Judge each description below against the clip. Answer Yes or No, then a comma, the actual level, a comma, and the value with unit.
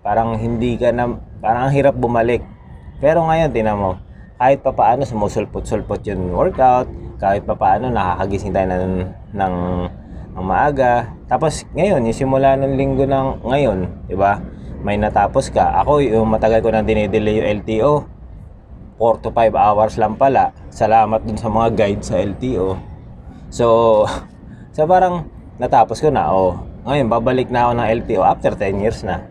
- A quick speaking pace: Yes, fast, 160 wpm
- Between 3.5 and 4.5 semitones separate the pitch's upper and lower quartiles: Yes, average, 3.8 semitones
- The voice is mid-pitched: No, low, 110 Hz